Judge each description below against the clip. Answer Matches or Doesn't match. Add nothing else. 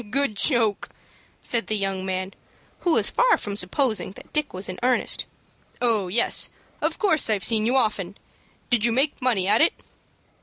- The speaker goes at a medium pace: Matches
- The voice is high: Matches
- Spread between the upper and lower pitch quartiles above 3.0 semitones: Matches